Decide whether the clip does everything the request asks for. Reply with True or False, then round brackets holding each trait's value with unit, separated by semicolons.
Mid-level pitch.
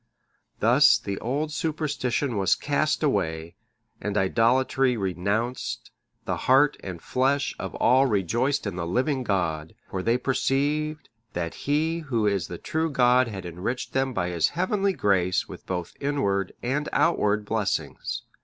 False (120 Hz)